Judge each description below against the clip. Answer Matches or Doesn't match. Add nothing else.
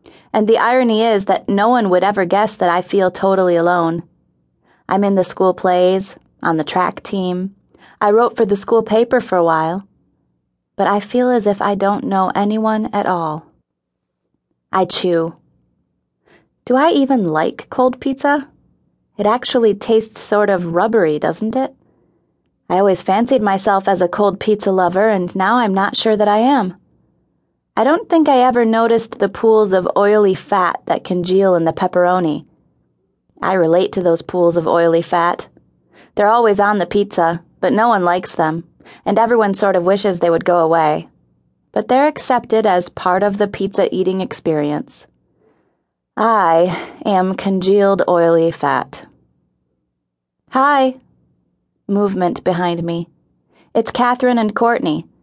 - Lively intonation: Doesn't match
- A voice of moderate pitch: Doesn't match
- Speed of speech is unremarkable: Matches